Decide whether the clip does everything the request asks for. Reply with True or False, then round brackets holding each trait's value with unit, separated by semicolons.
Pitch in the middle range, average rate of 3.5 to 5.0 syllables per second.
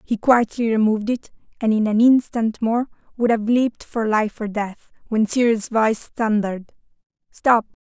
False (225 Hz; 4.6 syllables/s)